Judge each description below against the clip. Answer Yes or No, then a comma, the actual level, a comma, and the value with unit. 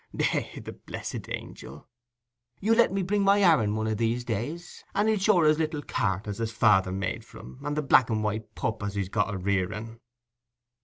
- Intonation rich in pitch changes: Yes, wide, 8.1 semitones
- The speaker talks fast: Yes, fast, 210 wpm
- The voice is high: No, low, 115 Hz